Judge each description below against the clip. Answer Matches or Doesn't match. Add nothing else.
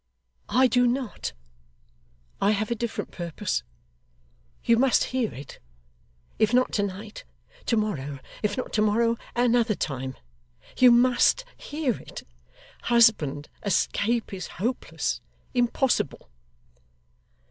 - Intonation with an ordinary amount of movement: Matches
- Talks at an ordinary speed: Doesn't match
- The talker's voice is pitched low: Doesn't match